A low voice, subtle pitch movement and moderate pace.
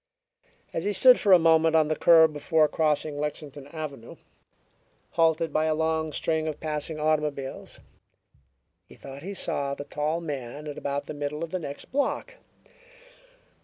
No: medium, 155 Hz; narrow, 1.8 semitones; average, 160 wpm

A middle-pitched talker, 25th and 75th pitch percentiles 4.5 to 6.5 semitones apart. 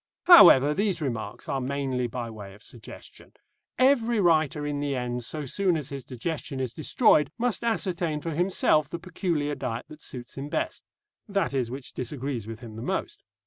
Yes: medium, 145 Hz; wide, 5.5 semitones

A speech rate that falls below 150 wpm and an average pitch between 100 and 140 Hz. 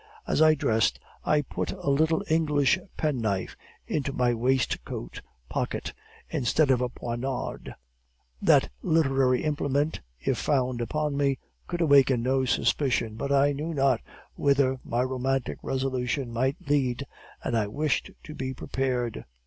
Yes: slow, 135 wpm; low, 135 Hz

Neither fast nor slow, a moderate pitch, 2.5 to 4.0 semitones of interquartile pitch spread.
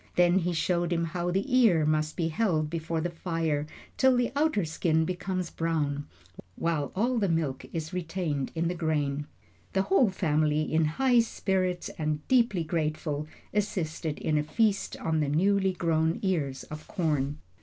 Yes: average, 165 wpm; medium, 165 Hz; average, 3.4 semitones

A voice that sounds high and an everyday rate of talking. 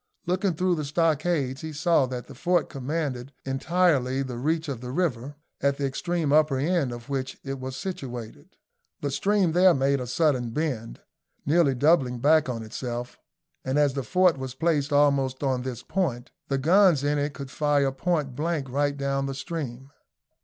No: medium, 140 Hz; average, 175 wpm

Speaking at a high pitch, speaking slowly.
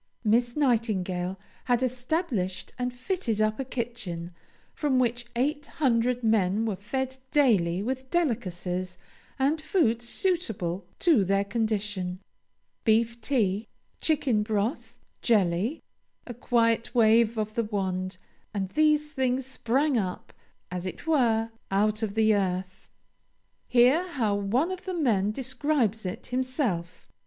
Yes: high, 230 Hz; slow, 125 wpm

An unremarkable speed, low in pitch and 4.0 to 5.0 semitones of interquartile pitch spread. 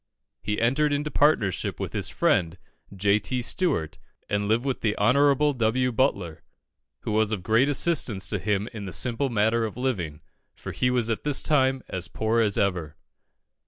Yes: average, 175 wpm; low, 110 Hz; average, 4.5 semitones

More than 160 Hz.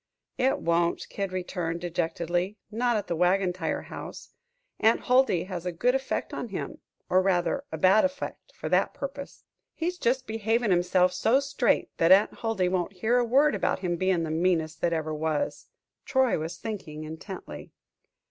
Yes: medium, 185 Hz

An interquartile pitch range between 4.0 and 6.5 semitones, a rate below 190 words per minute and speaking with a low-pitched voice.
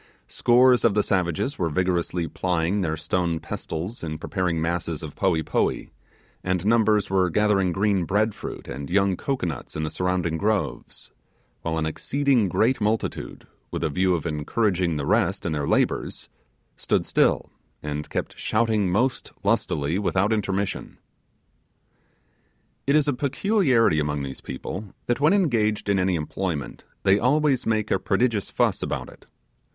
Yes: average, 5.0 semitones; average, 150 wpm; very low, 95 Hz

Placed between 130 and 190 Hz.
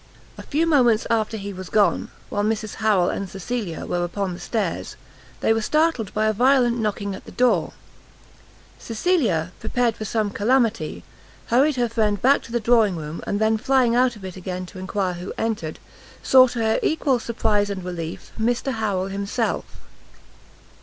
No: high, 220 Hz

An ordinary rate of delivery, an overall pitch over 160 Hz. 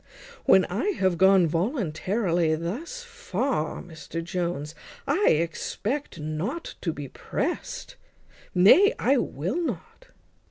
No: slow, 120 wpm; medium, 185 Hz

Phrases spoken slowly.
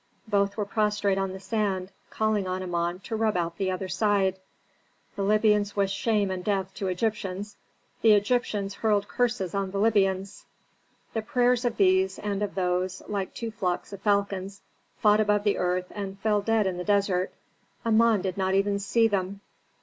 No: average, 175 wpm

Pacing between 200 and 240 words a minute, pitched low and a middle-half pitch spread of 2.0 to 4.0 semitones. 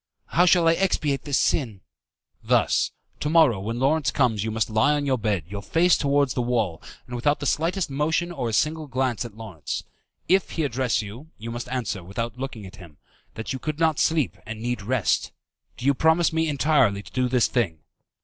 No: fast, 205 wpm; low, 130 Hz; wide, 5.4 semitones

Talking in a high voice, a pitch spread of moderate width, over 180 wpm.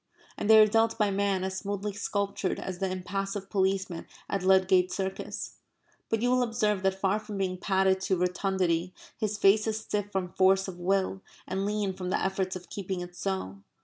No: high, 195 Hz; narrow, 1.5 semitones; average, 190 wpm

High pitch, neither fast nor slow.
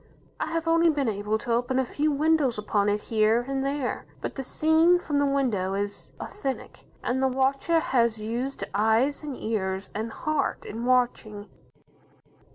Yes: very high, 255 Hz; average, 165 wpm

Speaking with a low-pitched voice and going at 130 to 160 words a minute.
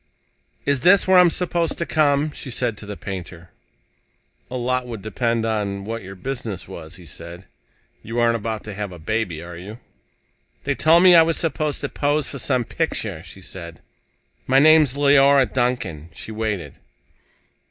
No: low, 115 Hz; average, 175 wpm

